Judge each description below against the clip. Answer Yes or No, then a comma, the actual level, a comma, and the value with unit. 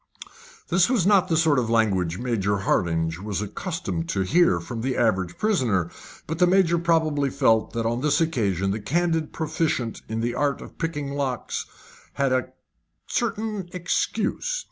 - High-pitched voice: No, low, 135 Hz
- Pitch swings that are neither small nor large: No, wide, 7.9 semitones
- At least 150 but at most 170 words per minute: Yes, average, 160 wpm